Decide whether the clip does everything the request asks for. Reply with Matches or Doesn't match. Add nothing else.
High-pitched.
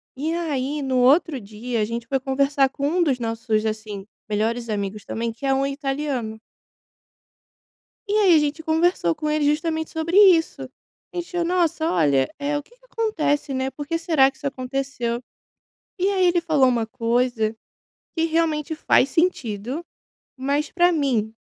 Matches